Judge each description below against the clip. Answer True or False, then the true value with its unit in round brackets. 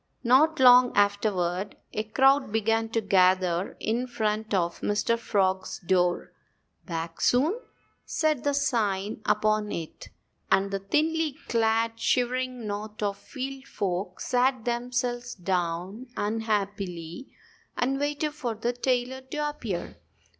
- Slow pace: True (120 wpm)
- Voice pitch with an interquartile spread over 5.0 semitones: False (4.5 semitones)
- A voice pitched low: False (225 Hz)